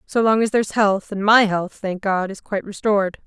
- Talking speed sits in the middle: No, fast, 240 wpm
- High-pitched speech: Yes, high, 205 Hz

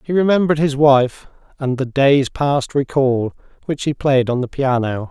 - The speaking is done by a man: Yes, male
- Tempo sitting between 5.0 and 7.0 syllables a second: No, 4.6 syllables/s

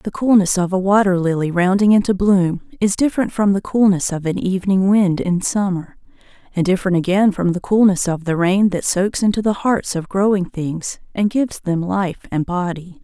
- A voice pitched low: No, high, 190 Hz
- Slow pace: No, average, 200 wpm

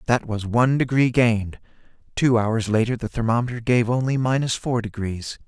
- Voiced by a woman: No, male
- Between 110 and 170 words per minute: Yes, average, 165 wpm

